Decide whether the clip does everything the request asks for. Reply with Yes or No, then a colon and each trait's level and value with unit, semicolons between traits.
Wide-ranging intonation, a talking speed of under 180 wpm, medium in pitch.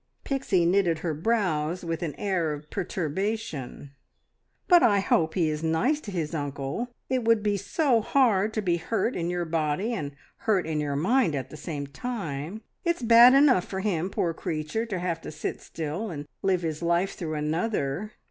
No: wide, 5.7 semitones; average, 185 wpm; medium, 175 Hz